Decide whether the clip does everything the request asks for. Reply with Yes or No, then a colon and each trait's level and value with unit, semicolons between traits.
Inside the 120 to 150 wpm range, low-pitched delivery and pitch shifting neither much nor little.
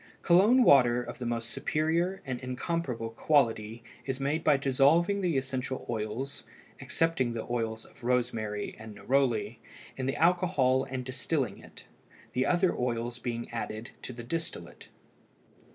Yes: average, 140 wpm; low, 130 Hz; average, 4.6 semitones